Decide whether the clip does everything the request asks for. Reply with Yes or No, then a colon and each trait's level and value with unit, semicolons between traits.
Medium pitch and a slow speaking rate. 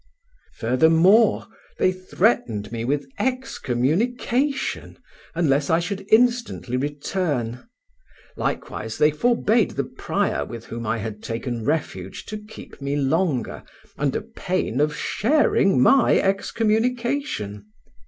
Yes: medium, 160 Hz; slow, 105 wpm